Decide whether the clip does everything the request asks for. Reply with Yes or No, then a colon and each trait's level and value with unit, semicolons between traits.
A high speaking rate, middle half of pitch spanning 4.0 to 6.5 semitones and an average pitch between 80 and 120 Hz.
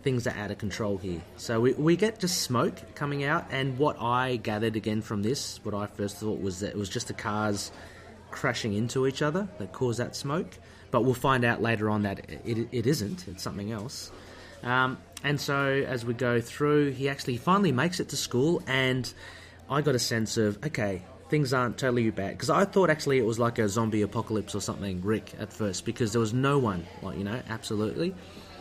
Yes: fast, 215 wpm; average, 4.5 semitones; low, 115 Hz